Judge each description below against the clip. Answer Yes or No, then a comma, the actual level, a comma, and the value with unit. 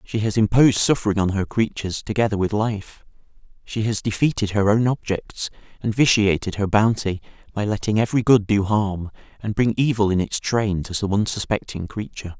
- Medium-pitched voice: No, low, 105 Hz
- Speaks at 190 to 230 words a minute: No, average, 175 wpm